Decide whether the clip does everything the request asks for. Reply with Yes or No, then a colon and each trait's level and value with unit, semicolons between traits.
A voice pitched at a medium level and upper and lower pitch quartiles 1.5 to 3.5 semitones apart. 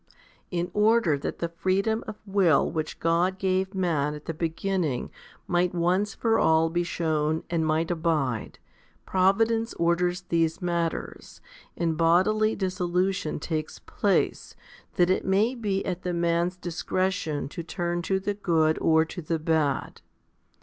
Yes: medium, 175 Hz; average, 2.8 semitones